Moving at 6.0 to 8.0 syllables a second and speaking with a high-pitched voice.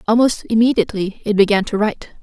Yes: 6.5 syllables/s; high, 215 Hz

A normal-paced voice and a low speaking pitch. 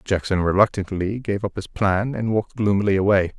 Yes: average, 175 wpm; low, 100 Hz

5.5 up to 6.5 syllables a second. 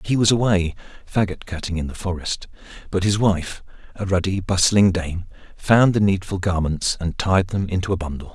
No: 5.1 syllables/s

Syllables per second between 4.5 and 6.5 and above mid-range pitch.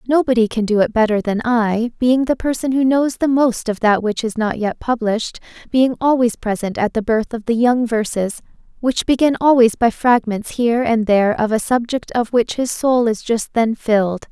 Yes: 5.0 syllables/s; high, 235 Hz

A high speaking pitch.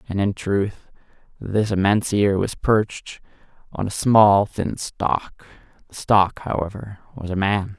No: low, 100 Hz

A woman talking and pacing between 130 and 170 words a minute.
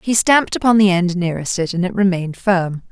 No: female; fast, 205 wpm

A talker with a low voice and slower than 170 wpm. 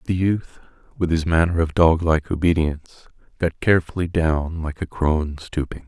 Yes: very low, 80 Hz; average, 155 wpm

